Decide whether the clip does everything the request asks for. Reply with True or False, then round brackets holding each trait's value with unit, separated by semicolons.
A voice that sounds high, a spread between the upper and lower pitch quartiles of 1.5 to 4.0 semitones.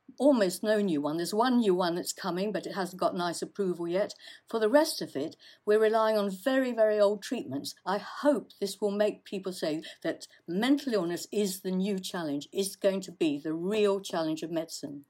True (200 Hz; 3.7 semitones)